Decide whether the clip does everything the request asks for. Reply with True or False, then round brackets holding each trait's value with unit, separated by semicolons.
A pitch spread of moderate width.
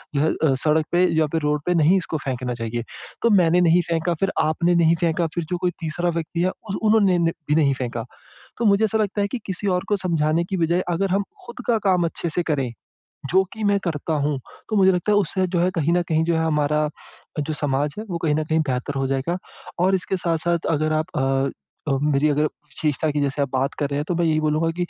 True (3.2 semitones)